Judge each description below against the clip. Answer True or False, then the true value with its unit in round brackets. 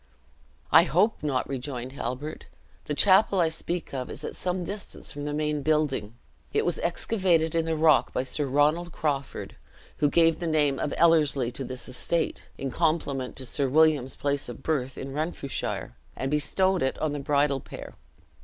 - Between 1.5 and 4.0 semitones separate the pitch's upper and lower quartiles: True (3.3 semitones)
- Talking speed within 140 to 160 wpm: False (175 wpm)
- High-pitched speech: False (150 Hz)